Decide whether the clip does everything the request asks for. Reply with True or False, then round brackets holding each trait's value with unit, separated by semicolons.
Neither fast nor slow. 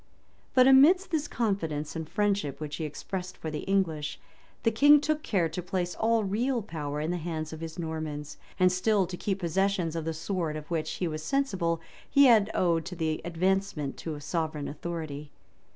True (185 wpm)